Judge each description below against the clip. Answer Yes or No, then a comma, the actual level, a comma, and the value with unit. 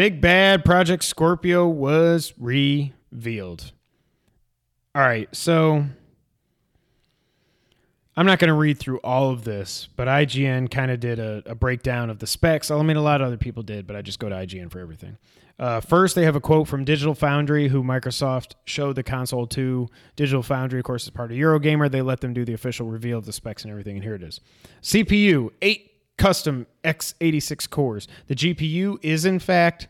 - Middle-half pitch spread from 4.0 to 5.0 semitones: Yes, average, 4.7 semitones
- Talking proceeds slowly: No, average, 190 wpm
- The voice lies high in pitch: No, low, 135 Hz